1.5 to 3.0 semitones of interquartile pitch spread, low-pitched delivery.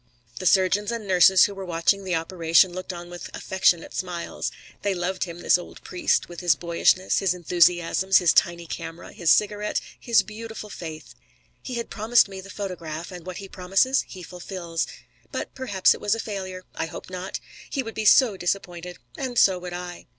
No: narrow, 2.5 semitones; medium, 185 Hz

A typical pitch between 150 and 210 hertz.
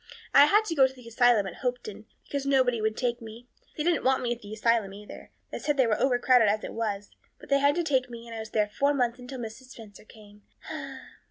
No: high, 245 Hz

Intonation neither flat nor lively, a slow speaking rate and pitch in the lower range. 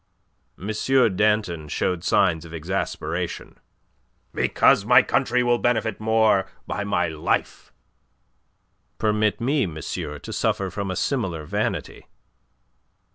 Yes: average, 4.5 semitones; slow, 110 wpm; low, 100 Hz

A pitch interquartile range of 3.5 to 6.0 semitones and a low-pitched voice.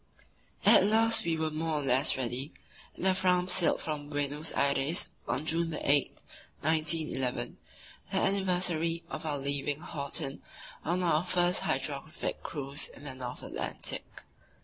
No: average, 3.8 semitones; medium, 155 Hz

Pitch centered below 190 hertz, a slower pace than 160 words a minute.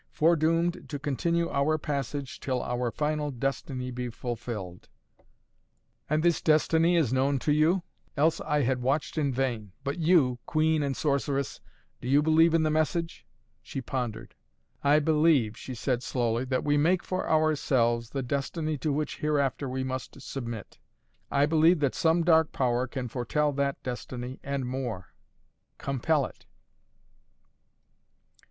Yes: medium, 140 Hz; average, 145 wpm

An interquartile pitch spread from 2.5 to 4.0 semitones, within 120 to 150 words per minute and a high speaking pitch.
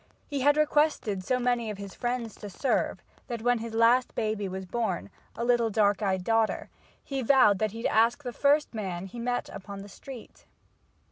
No: average, 3.4 semitones; average, 190 wpm; high, 230 Hz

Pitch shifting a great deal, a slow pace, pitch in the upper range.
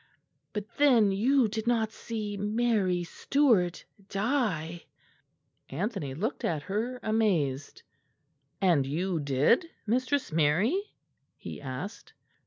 Yes: wide, 6.0 semitones; slow, 100 wpm; high, 205 Hz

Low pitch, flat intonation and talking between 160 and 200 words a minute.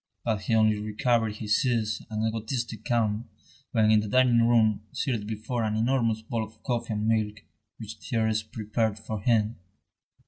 Yes: low, 110 Hz; narrow, 1.4 semitones; average, 165 wpm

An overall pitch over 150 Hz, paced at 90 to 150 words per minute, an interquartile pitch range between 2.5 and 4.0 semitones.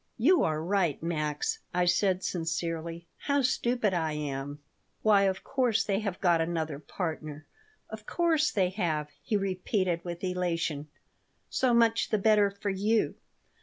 No: medium, 185 Hz; average, 145 wpm; average, 4.5 semitones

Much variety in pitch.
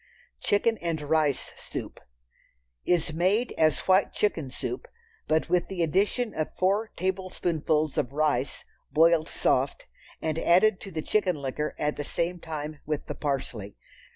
No: average, 3.7 semitones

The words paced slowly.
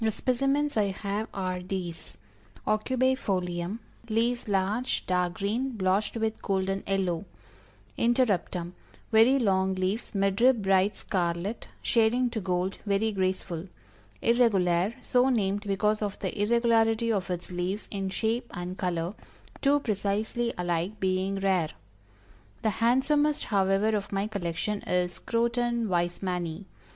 Yes: slow, 125 wpm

